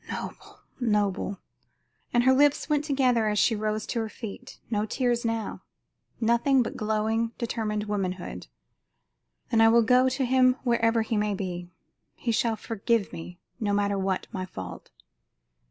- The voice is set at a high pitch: Yes, high, 225 Hz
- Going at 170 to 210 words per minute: No, average, 155 wpm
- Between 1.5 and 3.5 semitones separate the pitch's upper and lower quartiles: Yes, narrow, 2.6 semitones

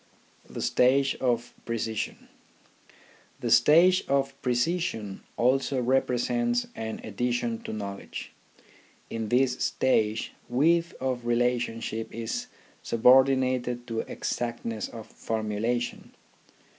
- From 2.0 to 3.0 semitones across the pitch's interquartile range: Yes, average, 2.7 semitones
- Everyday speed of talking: No, slow, 100 wpm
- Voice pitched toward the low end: Yes, low, 120 Hz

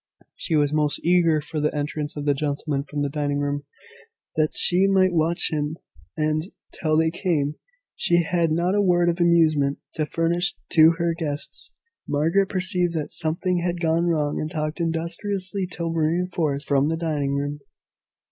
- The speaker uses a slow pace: No, average, 165 wpm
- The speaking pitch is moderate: Yes, medium, 160 Hz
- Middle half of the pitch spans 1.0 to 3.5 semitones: Yes, average, 2.7 semitones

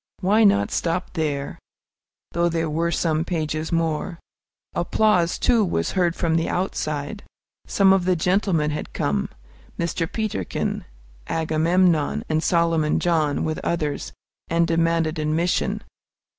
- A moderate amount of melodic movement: No, narrow, 2.3 semitones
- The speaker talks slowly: Yes, slow, 125 wpm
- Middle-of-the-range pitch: Yes, medium, 165 Hz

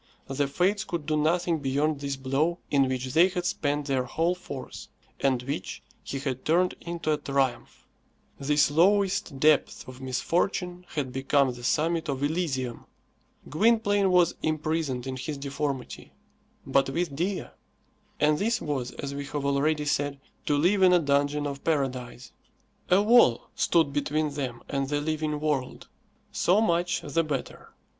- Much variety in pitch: No, average, 3.7 semitones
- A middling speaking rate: Yes, average, 155 wpm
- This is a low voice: No, medium, 150 Hz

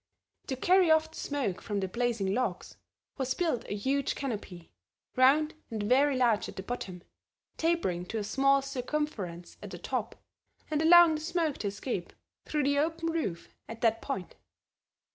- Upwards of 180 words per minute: No, average, 165 wpm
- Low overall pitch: No, very high, 255 Hz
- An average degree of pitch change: No, wide, 6.8 semitones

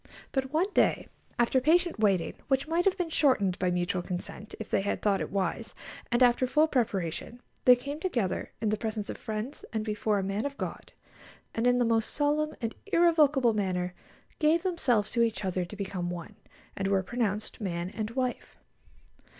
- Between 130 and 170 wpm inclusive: No, average, 185 wpm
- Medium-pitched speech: No, high, 225 Hz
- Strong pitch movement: Yes, wide, 6.1 semitones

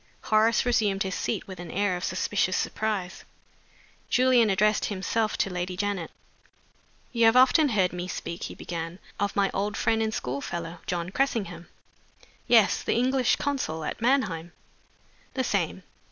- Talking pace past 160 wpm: No, average, 155 wpm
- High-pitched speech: Yes, high, 200 Hz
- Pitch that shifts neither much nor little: Yes, average, 4.2 semitones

